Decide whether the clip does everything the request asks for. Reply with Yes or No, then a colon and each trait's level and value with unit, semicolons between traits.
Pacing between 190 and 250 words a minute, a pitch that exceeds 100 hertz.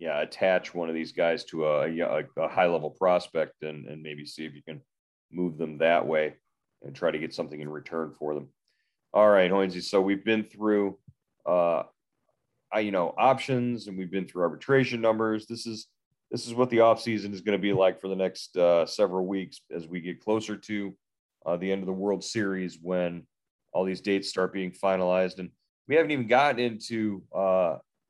No: average, 200 wpm; very low, 95 Hz